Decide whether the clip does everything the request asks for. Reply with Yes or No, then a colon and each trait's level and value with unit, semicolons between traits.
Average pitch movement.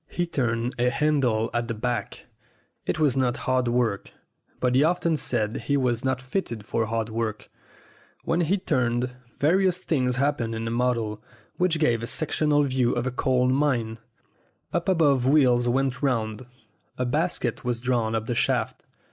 Yes: average, 3.7 semitones